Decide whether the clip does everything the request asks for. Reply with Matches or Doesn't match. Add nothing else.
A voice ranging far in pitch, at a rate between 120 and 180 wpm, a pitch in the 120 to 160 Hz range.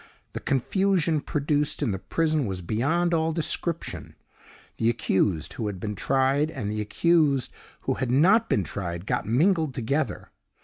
Matches